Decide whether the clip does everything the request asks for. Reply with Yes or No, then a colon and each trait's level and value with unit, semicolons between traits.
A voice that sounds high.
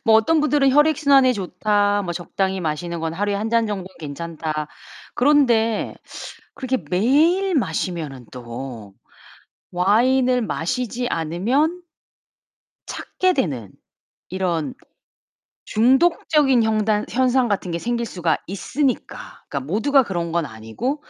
Yes: high, 210 Hz